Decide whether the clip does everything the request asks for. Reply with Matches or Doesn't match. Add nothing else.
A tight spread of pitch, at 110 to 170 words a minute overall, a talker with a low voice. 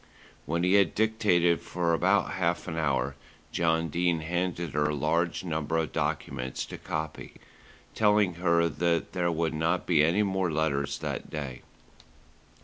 Matches